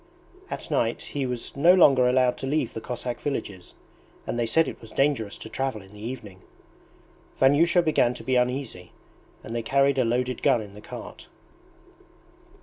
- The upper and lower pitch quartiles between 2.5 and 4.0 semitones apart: Yes, average, 3.4 semitones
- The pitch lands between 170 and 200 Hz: No, low, 125 Hz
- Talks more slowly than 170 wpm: No, average, 175 wpm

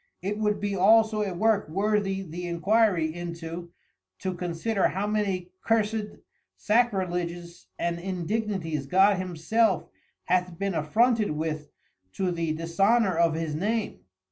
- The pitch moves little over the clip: No, average, 3.7 semitones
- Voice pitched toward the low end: No, medium, 185 Hz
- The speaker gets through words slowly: Yes, slow, 125 wpm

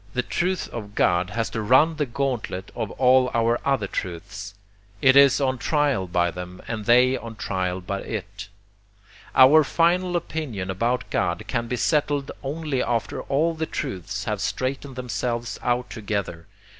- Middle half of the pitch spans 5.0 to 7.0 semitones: Yes, average, 5.3 semitones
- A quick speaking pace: No, average, 155 wpm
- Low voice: Yes, low, 120 Hz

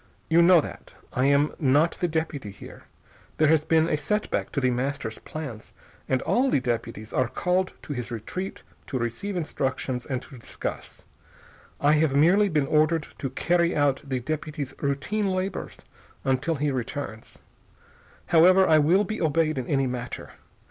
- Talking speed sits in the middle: Yes, average, 165 wpm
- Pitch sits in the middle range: Yes, medium, 150 Hz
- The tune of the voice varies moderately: Yes, average, 4.3 semitones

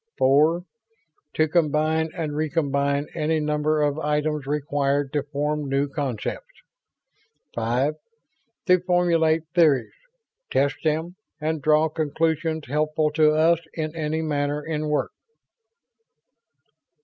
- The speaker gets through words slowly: Yes, slow, 110 wpm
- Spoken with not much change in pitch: Yes, narrow, 1.7 semitones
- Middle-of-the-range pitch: Yes, medium, 150 Hz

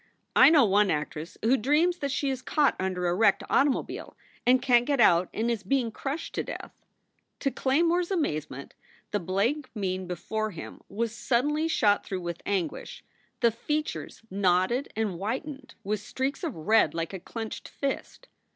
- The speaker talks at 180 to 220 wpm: No, average, 170 wpm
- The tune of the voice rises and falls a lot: Yes, wide, 6.6 semitones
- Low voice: No, high, 225 Hz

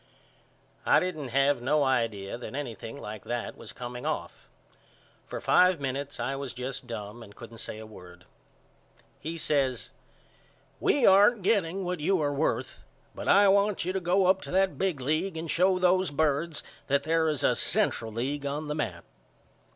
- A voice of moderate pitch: Yes, medium, 145 Hz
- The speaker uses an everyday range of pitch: No, wide, 6.7 semitones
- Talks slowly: No, average, 175 wpm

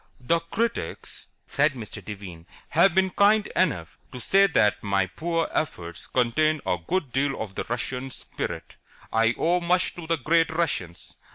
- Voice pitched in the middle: Yes, medium, 145 Hz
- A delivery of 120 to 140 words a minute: No, average, 160 wpm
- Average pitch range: No, wide, 7.8 semitones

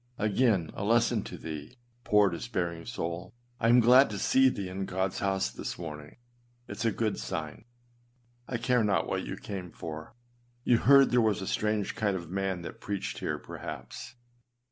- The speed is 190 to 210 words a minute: No, average, 180 wpm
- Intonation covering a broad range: No, average, 4.3 semitones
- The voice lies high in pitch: No, low, 100 Hz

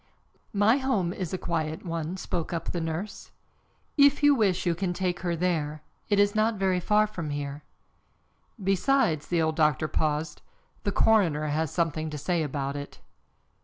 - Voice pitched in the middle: Yes, medium, 170 Hz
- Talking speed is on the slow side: No, average, 165 wpm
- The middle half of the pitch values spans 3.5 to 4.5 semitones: Yes, average, 4.2 semitones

